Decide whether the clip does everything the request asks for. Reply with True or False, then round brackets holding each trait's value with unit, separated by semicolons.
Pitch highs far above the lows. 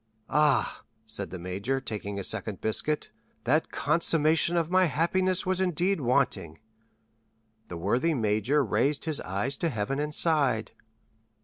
True (7.2 semitones)